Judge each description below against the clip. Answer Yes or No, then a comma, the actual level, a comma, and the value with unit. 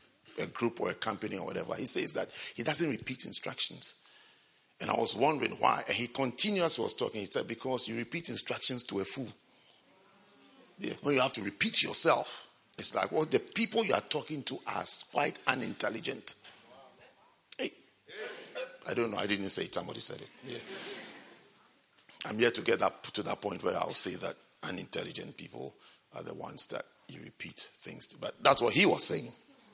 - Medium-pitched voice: No, low, 130 Hz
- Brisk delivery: No, average, 190 wpm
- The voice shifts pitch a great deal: Yes, wide, 8.4 semitones